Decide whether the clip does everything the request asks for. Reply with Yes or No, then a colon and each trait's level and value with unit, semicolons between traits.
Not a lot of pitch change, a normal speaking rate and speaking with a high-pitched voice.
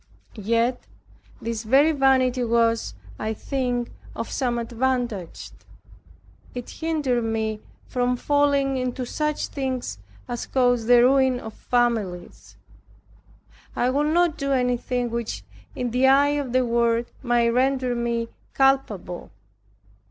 No: narrow, 2.3 semitones; slow, 120 wpm; high, 245 Hz